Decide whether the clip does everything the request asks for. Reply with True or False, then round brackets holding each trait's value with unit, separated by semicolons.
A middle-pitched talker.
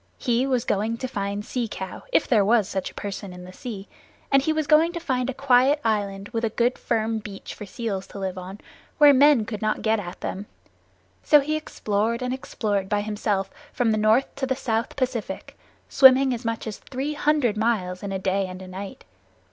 False (225 Hz)